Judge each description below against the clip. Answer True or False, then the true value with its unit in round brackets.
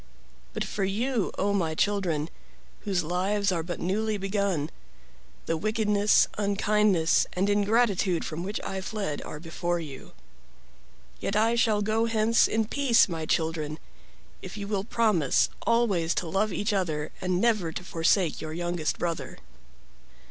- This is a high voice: True (195 Hz)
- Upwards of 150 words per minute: False (145 wpm)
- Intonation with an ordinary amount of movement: True (4.1 semitones)